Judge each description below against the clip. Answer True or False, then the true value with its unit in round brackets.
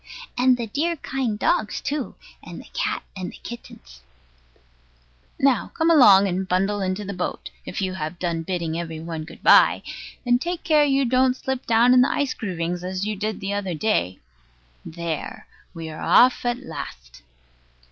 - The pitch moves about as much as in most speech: False (6.6 semitones)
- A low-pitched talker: False (200 Hz)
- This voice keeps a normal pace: True (175 wpm)